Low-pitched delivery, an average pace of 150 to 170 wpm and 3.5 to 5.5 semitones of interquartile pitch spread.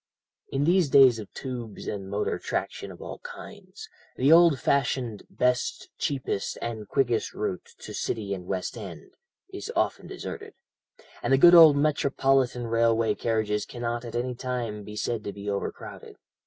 Yes: low, 120 Hz; average, 155 wpm; average, 4.3 semitones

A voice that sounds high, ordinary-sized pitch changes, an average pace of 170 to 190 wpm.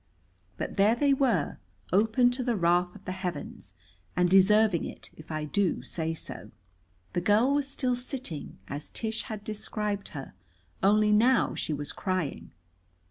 No: high, 205 Hz; average, 4.8 semitones; average, 155 wpm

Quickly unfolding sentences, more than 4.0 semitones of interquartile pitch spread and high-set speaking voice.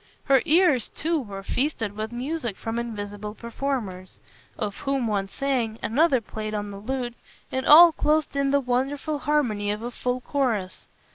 No: average, 160 wpm; average, 4.7 semitones; high, 245 Hz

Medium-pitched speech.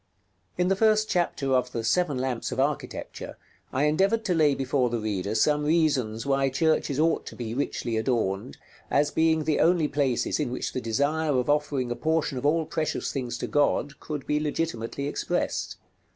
Yes: medium, 145 Hz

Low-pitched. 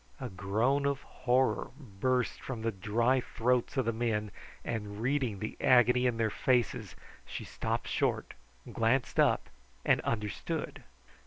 Yes: low, 120 Hz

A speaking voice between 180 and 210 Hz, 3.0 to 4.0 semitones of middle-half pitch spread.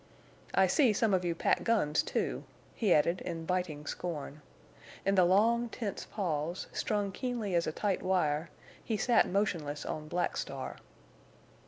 No: medium, 185 Hz; average, 4.5 semitones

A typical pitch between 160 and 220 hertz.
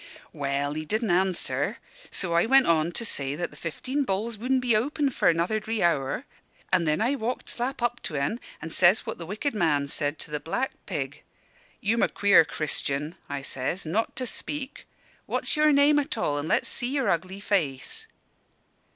Yes: high, 190 Hz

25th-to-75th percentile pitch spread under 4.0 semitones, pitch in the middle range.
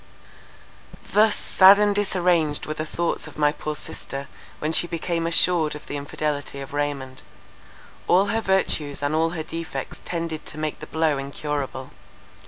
Yes: average, 3.0 semitones; medium, 155 Hz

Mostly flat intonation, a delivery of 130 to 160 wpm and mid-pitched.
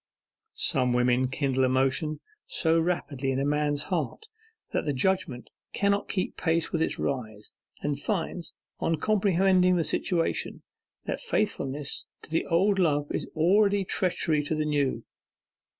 No: average, 5.0 semitones; average, 140 wpm; medium, 155 Hz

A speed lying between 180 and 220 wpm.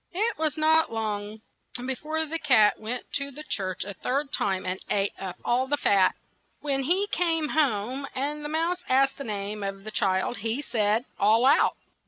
Yes: average, 190 wpm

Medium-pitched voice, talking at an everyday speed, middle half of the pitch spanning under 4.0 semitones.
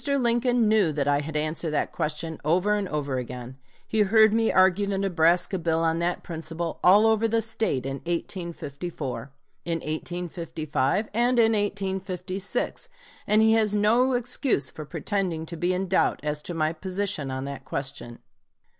No: medium, 180 Hz; average, 165 wpm; average, 5.2 semitones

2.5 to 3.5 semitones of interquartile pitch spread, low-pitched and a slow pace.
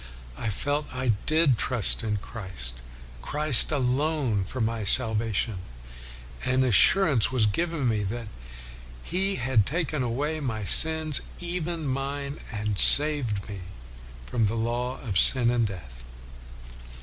No: wide, 5.5 semitones; low, 125 Hz; slow, 125 wpm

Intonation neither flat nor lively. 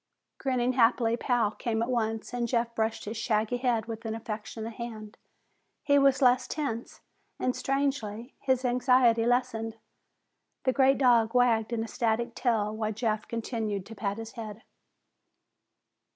No: narrow, 2.0 semitones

